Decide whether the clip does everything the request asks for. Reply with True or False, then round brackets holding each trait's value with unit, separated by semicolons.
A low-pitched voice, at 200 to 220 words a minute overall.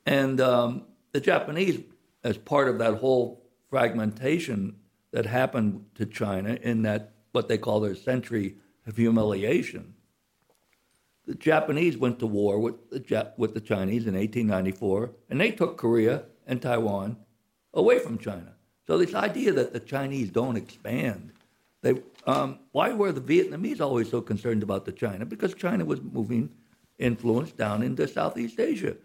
False (115 Hz; 155 wpm)